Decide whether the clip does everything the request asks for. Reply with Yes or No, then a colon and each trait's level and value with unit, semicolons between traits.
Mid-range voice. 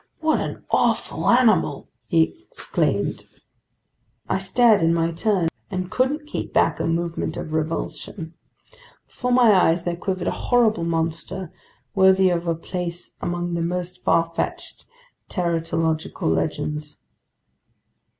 Yes: medium, 175 Hz